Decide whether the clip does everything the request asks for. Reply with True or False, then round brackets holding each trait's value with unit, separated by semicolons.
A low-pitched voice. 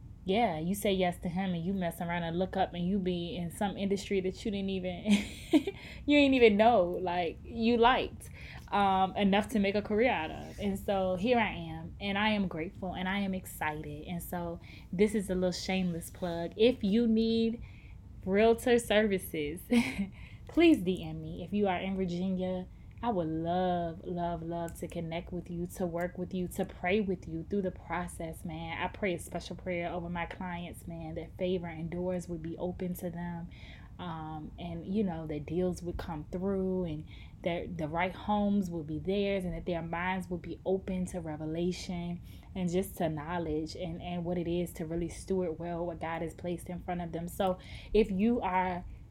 False (180 Hz)